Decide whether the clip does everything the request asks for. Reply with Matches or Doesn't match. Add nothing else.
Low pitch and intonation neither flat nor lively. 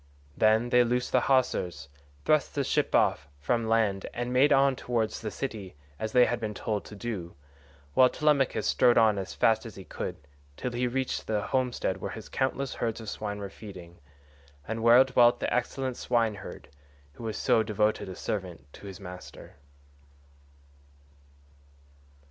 Matches